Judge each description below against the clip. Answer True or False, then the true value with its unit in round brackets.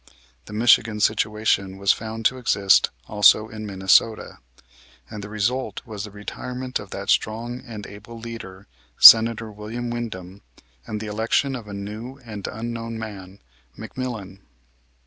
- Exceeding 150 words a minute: False (140 wpm)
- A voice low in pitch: True (110 Hz)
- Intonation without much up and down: True (2.2 semitones)